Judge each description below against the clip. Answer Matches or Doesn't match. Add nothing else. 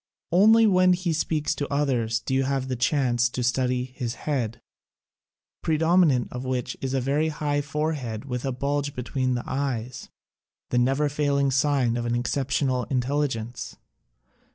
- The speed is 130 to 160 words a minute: Matches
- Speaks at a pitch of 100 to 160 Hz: Matches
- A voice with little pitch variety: Doesn't match